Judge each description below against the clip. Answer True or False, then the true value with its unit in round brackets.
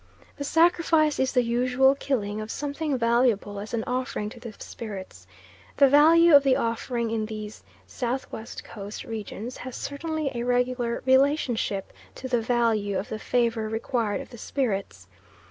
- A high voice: True (240 Hz)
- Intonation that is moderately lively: True (3.6 semitones)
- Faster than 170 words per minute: False (155 wpm)